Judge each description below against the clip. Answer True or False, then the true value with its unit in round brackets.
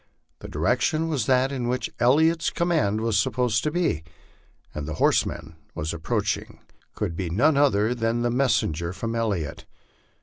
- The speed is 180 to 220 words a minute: False (145 wpm)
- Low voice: True (115 Hz)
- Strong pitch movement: True (6.3 semitones)